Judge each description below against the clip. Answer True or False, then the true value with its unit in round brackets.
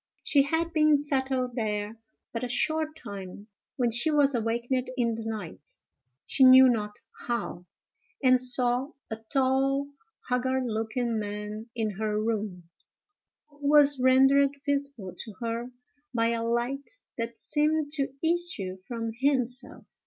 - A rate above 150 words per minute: False (135 wpm)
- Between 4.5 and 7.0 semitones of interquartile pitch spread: False (3.8 semitones)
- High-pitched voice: True (250 Hz)